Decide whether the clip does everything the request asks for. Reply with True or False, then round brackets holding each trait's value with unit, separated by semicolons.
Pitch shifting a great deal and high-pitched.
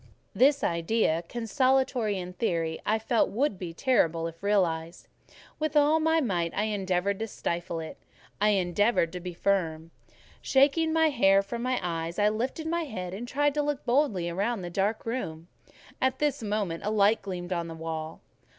True (6.8 semitones; 205 Hz)